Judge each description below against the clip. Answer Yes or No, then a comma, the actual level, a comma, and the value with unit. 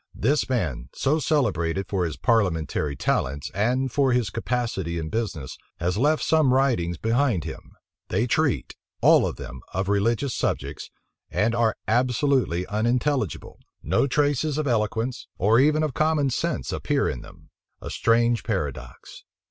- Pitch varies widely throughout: Yes, wide, 6.6 semitones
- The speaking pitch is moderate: No, low, 115 Hz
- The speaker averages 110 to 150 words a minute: Yes, average, 145 wpm